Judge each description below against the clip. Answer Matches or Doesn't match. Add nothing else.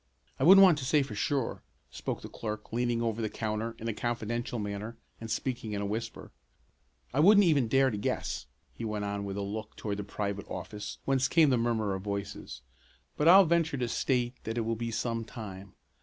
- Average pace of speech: Doesn't match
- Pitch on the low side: Matches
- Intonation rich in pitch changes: Doesn't match